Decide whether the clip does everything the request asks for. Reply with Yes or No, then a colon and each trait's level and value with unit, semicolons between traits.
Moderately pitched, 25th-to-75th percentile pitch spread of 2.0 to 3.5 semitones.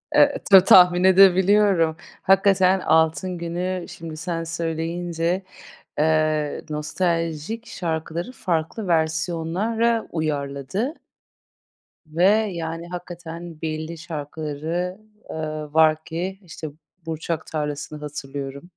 Yes: medium, 165 Hz; narrow, 2.5 semitones